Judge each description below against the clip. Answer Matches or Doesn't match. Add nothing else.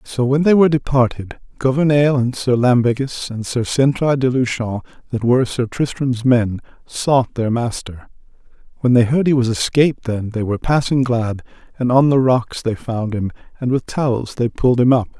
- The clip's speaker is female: Doesn't match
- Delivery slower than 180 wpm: Doesn't match